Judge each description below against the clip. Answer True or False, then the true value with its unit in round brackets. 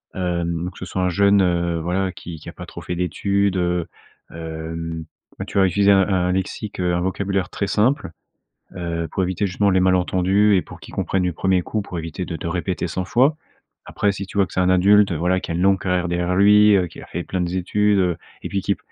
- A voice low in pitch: True (90 Hz)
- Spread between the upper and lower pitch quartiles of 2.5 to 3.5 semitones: False (2.1 semitones)